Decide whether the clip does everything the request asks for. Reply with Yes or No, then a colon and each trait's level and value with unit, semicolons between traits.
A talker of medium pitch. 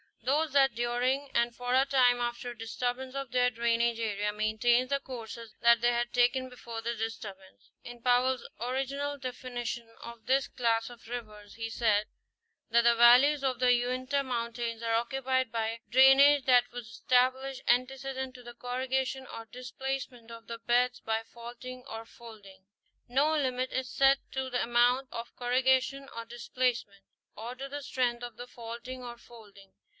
No: high, 245 Hz